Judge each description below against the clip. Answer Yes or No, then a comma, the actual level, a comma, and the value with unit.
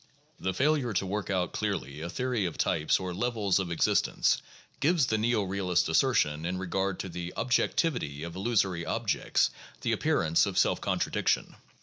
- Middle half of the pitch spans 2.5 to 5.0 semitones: No, wide, 5.4 semitones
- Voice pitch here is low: Yes, very low, 95 Hz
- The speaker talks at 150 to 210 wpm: Yes, average, 160 wpm